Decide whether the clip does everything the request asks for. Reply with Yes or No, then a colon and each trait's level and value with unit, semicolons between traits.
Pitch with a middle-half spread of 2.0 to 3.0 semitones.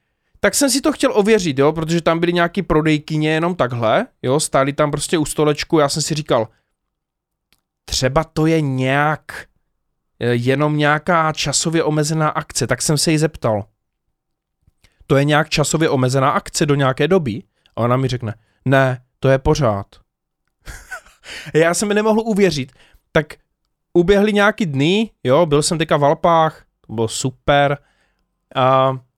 No: average, 3.8 semitones